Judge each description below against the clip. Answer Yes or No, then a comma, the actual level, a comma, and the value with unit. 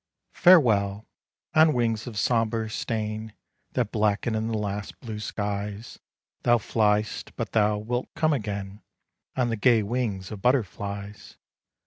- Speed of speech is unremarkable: No, slow, 130 wpm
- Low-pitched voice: Yes, low, 110 Hz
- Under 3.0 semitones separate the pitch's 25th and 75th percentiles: Yes, narrow, 2.6 semitones